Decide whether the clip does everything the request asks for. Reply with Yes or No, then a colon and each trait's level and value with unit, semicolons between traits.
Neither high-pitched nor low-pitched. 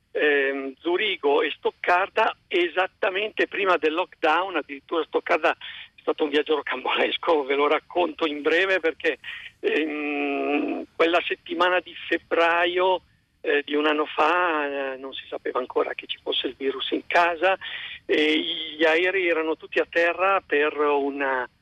Yes: medium, 170 Hz